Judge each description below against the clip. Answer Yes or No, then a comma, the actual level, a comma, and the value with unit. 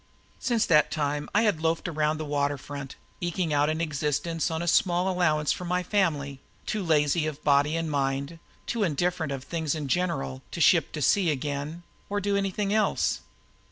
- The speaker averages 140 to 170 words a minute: No, average, 185 wpm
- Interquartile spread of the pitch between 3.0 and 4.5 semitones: Yes, average, 3.6 semitones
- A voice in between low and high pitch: Yes, medium, 155 Hz